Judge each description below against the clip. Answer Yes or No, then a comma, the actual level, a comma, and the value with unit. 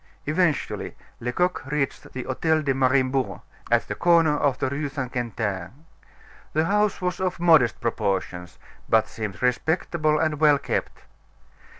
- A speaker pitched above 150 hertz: No, medium, 140 Hz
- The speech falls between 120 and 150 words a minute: Yes, slow, 135 wpm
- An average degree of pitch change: Yes, average, 4.5 semitones